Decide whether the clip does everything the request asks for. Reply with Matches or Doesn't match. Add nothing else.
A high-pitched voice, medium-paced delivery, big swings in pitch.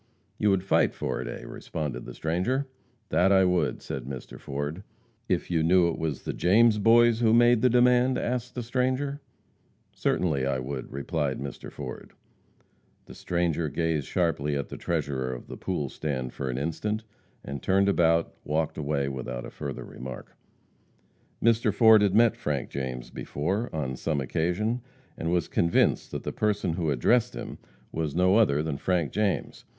Doesn't match